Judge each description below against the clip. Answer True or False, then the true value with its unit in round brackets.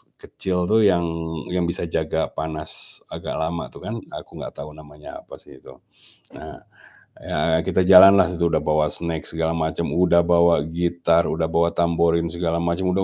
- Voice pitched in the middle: False (85 Hz)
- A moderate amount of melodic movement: False (1.4 semitones)